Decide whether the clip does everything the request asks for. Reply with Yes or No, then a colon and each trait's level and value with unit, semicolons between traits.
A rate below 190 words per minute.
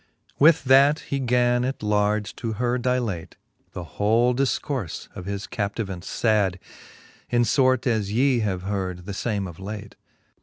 Yes: average, 150 wpm